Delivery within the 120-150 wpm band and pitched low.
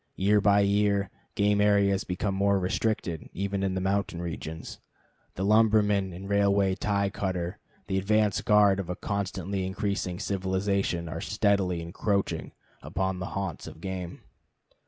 Yes: average, 140 wpm; low, 100 Hz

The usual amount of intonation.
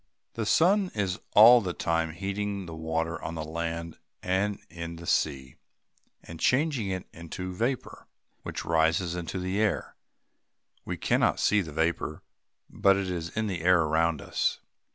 Yes: average, 3.6 semitones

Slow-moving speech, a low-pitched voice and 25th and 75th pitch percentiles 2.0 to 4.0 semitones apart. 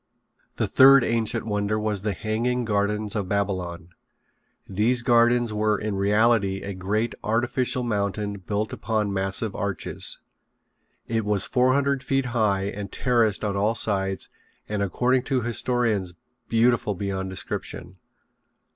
Yes: slow, 130 wpm; low, 105 Hz; average, 2.9 semitones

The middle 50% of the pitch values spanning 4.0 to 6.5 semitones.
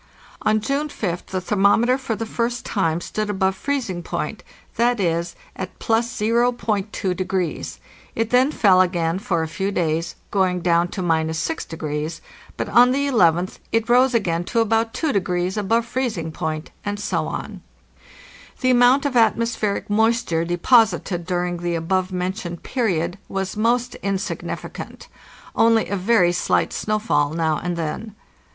Yes: average, 4.9 semitones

